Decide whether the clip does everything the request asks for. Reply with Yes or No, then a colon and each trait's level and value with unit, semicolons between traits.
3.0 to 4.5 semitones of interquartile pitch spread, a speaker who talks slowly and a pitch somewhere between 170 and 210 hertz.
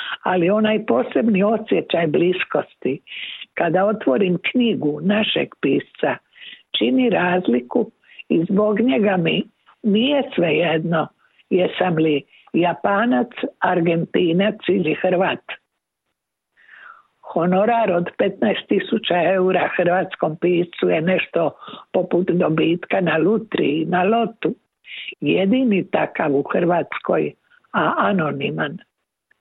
Yes: average, 4.2 semitones; slow, 95 wpm; high, 190 Hz